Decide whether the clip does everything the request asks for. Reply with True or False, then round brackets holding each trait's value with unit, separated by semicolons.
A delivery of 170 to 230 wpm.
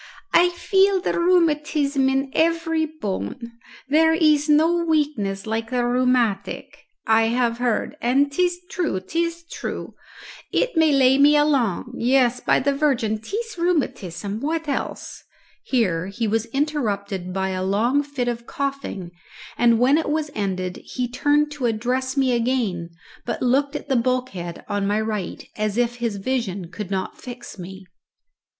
False (150 wpm)